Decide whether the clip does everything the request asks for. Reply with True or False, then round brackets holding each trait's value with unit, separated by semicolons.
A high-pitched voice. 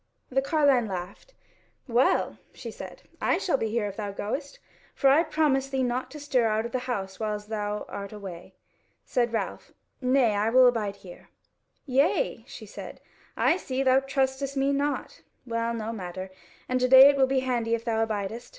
True (245 Hz)